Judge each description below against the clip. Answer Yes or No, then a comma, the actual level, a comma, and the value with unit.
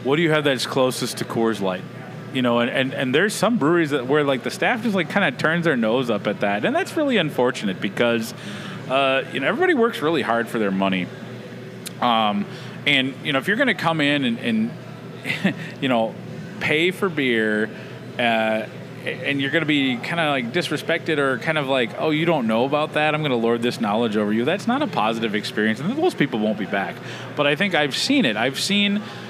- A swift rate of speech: Yes, fast, 220 wpm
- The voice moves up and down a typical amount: No, wide, 6.7 semitones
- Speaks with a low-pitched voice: No, medium, 145 Hz